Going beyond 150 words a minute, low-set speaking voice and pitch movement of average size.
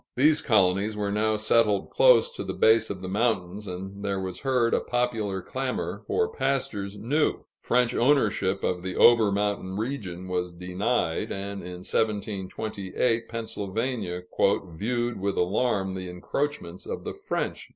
No: average, 145 wpm; low, 105 Hz; average, 4.1 semitones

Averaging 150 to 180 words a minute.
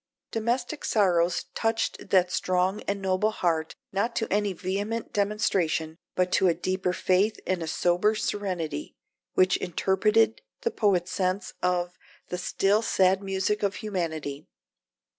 No: slow, 135 wpm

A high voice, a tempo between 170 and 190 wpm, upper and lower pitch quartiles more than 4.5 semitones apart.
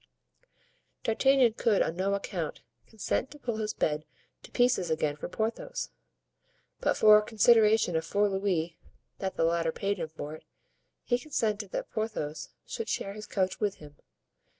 No: high, 200 Hz; average, 160 wpm; average, 5.1 semitones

